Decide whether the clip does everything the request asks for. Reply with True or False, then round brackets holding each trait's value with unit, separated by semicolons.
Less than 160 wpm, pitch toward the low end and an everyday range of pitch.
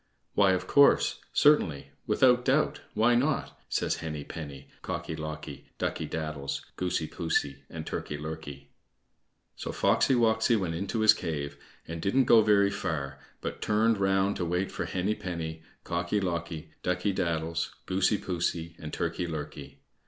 True (150 wpm; 85 Hz; 4.7 semitones)